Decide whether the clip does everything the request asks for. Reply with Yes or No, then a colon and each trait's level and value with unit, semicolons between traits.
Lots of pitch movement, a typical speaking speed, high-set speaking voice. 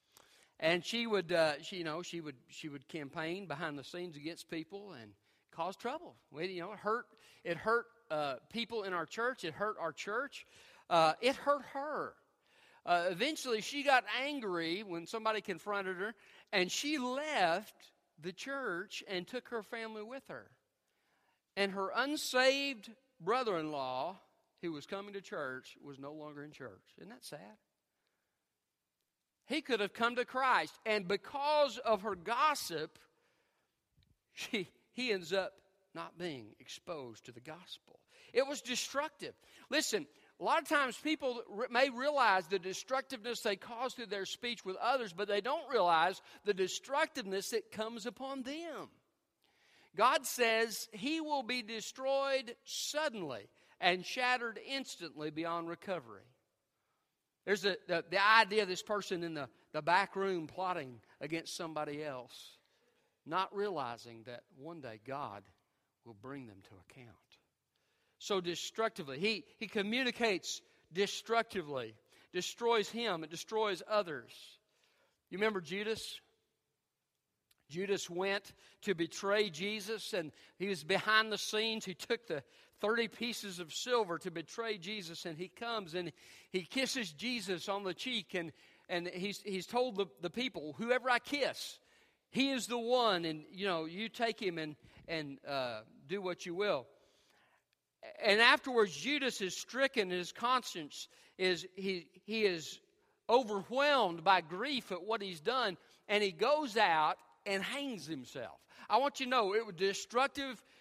Yes: wide, 5.9 semitones; average, 150 wpm; high, 205 Hz